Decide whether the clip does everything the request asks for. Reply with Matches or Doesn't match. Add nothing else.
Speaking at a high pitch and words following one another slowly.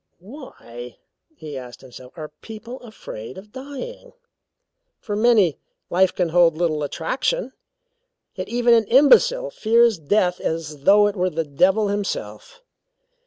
Matches